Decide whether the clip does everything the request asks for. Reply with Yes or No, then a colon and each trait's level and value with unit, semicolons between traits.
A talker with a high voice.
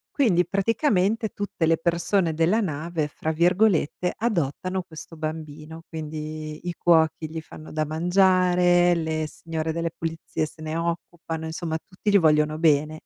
No: medium, 165 Hz